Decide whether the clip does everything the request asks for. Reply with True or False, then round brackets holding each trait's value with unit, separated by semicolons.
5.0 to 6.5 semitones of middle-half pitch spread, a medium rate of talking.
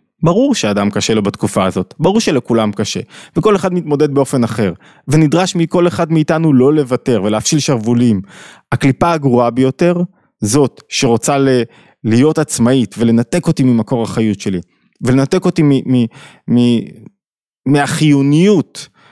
True (5.4 semitones; 130 wpm)